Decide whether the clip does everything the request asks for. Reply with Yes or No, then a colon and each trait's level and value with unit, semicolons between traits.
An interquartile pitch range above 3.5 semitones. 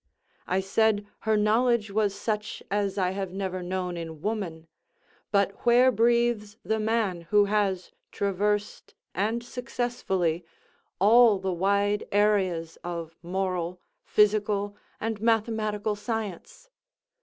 No: average, 2.7 semitones